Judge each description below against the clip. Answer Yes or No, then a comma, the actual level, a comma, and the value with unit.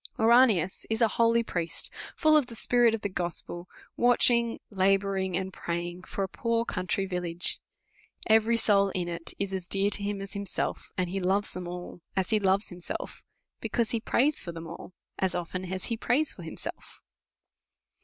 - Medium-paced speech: Yes, average, 180 wpm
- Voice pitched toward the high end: Yes, high, 195 Hz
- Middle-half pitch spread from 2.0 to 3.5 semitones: No, average, 4.1 semitones